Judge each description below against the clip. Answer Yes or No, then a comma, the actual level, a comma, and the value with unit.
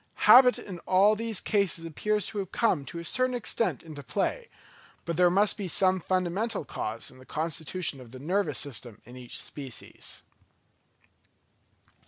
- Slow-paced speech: No, average, 160 wpm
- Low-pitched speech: No, medium, 180 Hz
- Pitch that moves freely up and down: Yes, wide, 6.3 semitones